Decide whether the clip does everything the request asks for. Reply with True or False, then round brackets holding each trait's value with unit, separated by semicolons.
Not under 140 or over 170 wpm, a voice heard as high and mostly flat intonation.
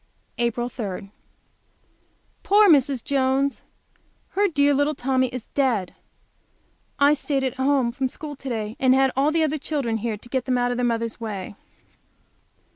False (160 wpm; 260 Hz; 3.1 semitones)